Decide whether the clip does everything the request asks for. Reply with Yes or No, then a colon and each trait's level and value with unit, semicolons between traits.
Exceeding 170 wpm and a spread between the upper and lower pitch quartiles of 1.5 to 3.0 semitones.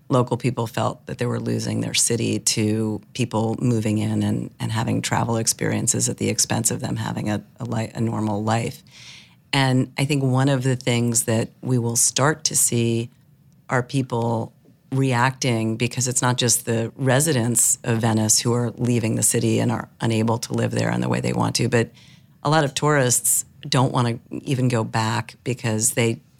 Yes: average, 190 wpm; narrow, 2.6 semitones